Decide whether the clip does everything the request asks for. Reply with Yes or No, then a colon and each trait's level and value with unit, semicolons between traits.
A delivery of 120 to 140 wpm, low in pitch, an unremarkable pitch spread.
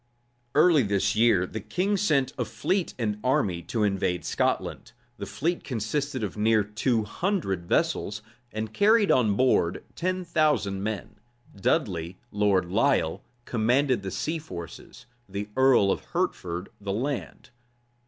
No: slow, 135 wpm; low, 110 Hz; wide, 6.2 semitones